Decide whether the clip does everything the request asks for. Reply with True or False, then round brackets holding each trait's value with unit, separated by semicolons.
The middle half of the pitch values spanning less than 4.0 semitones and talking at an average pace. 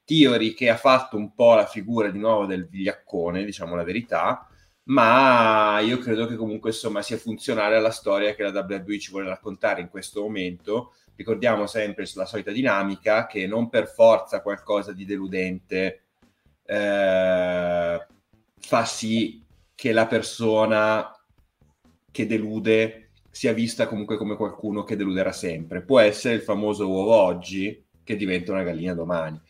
True (2.7 semitones; 150 wpm)